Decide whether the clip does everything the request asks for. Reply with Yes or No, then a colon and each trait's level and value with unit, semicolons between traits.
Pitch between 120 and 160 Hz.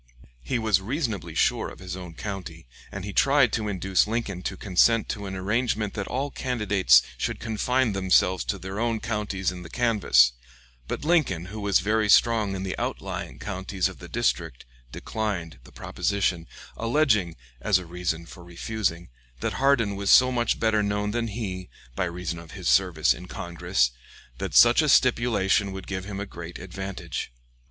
No: low, 100 Hz